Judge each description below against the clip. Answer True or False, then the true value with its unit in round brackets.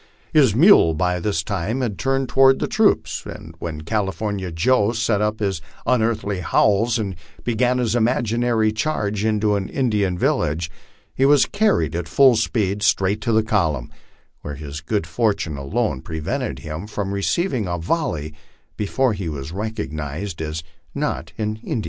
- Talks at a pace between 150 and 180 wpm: True (160 wpm)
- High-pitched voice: False (105 Hz)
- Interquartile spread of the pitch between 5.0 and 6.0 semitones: True (5.6 semitones)